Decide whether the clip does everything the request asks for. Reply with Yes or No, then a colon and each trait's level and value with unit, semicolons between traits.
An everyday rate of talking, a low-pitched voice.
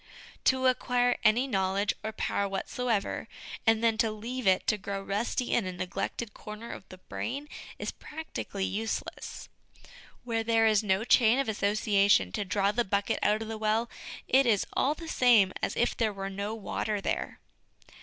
No: average, 175 wpm; high, 215 Hz